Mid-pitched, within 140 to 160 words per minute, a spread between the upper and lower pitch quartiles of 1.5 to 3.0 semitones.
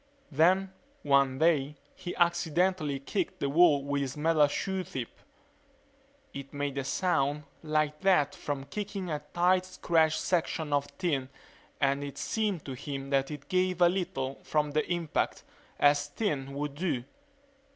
No: medium, 150 Hz; average, 145 wpm; average, 4.1 semitones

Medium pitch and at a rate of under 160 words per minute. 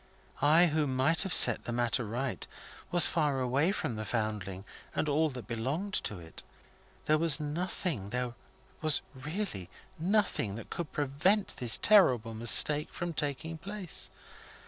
Yes: medium, 145 Hz; average, 145 wpm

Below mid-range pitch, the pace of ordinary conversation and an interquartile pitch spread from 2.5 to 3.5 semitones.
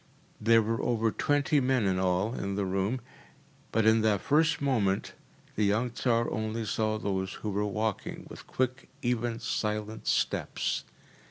Yes: low, 110 Hz; average, 155 wpm; average, 2.8 semitones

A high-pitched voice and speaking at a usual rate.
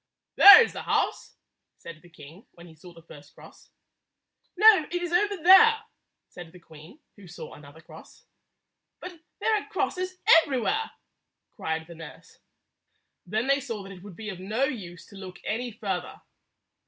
Yes: high, 205 Hz; average, 165 wpm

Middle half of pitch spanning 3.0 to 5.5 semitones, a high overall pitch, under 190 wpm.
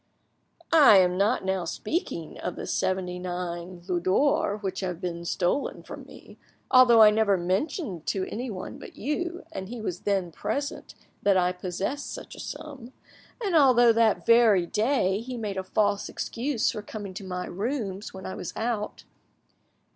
Yes: average, 4.6 semitones; high, 205 Hz; average, 165 wpm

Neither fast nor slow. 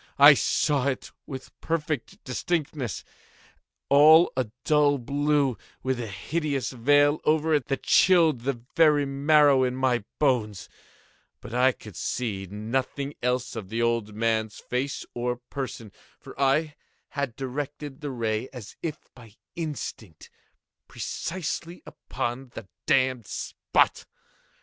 No: slow, 125 wpm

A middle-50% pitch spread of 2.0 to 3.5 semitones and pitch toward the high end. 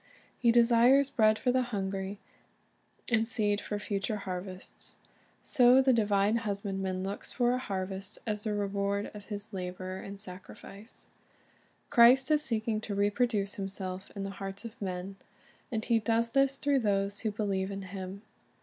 Yes: average, 3.0 semitones; high, 205 Hz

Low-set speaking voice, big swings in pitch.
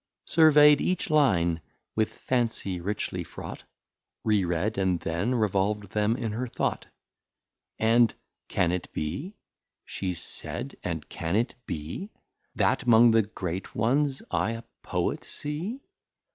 Yes: low, 110 Hz; wide, 5.7 semitones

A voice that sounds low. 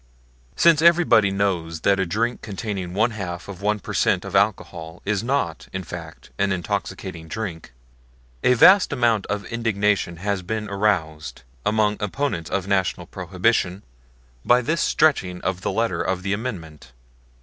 Yes: low, 100 Hz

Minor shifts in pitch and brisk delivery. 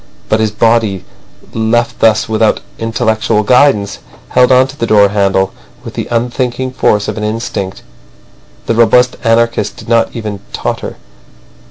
No: narrow, 2.0 semitones; average, 145 wpm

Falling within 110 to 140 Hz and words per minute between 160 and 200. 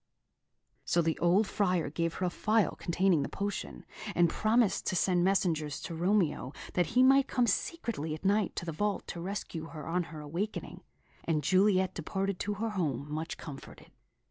No: medium, 180 Hz; average, 175 wpm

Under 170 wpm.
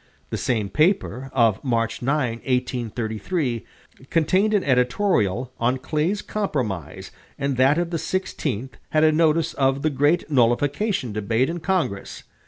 Yes: slow, 135 wpm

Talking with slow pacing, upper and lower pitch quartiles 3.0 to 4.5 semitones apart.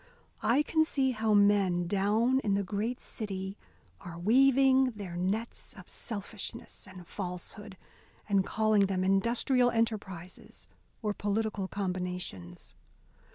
Yes: slow, 115 wpm; average, 3.4 semitones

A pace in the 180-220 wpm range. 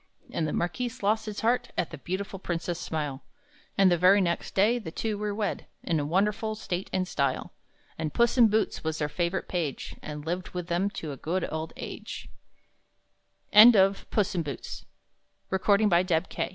Yes: average, 190 wpm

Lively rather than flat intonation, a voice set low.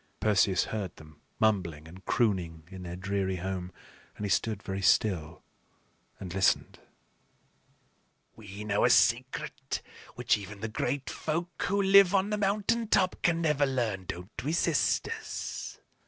Yes: wide, 9.0 semitones; low, 105 Hz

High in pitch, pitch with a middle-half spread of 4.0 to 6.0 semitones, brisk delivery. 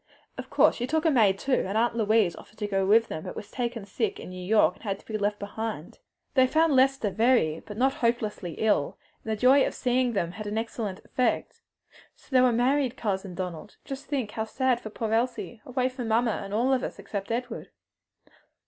No: high, 225 Hz; average, 3.6 semitones; fast, 220 wpm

